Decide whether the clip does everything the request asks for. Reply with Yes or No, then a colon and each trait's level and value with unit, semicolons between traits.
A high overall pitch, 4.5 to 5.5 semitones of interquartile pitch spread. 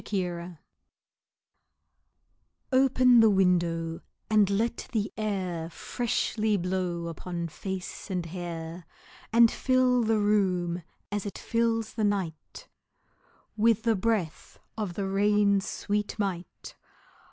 No: high, 200 Hz; average, 3.8 semitones